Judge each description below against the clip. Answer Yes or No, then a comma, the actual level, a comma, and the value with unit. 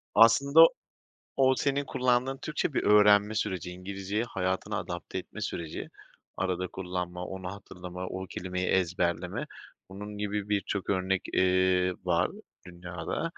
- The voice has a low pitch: Yes, very low, 95 Hz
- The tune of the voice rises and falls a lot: No, narrow, 2.4 semitones